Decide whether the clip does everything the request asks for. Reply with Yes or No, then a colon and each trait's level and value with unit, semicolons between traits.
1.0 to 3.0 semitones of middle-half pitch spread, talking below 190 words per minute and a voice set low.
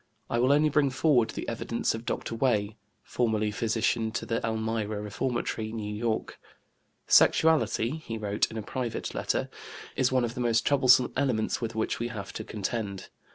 Yes: narrow, 2.4 semitones; average, 170 wpm; low, 115 Hz